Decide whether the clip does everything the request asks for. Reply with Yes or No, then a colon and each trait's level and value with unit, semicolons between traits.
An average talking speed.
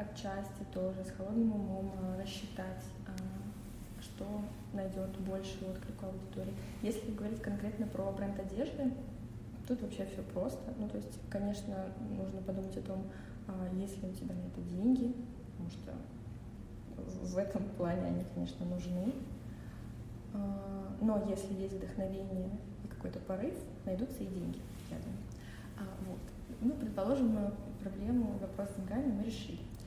Yes: average, 130 wpm